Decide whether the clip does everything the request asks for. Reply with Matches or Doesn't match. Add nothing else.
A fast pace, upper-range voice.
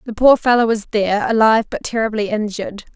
Doesn't match